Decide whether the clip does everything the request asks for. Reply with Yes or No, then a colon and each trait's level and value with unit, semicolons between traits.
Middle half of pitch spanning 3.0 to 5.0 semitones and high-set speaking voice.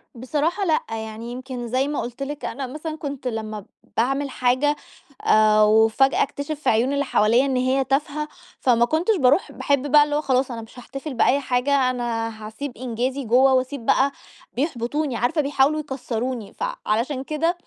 Yes: average, 3.3 semitones; very high, 260 Hz